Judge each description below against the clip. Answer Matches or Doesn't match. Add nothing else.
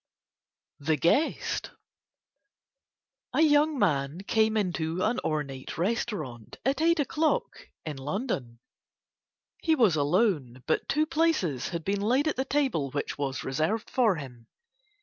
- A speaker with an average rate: Doesn't match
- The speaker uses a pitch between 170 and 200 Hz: Matches